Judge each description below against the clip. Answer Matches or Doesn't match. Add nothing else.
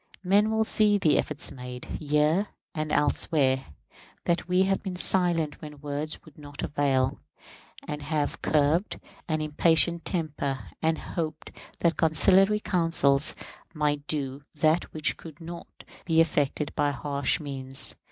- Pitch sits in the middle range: Matches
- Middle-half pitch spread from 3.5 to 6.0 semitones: Doesn't match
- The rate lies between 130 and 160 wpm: Matches